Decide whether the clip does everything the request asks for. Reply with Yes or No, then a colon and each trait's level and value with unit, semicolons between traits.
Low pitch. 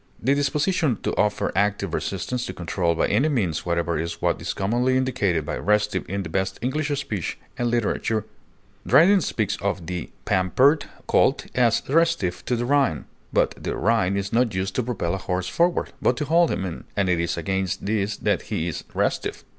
Yes: low, 105 Hz